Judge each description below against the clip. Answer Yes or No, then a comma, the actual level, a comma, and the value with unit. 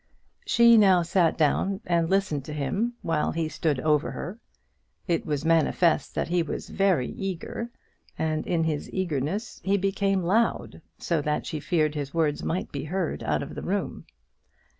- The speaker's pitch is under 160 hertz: No, medium, 165 Hz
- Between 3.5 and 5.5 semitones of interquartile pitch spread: Yes, average, 4.0 semitones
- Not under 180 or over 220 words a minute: No, average, 165 wpm